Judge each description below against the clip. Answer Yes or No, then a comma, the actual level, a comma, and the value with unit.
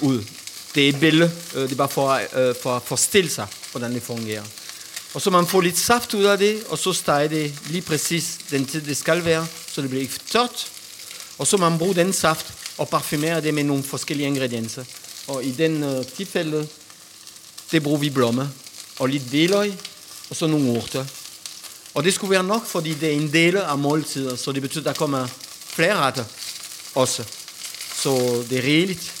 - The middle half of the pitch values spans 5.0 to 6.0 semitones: No, average, 4.2 semitones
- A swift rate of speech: No, average, 195 wpm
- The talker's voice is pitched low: No, medium, 150 Hz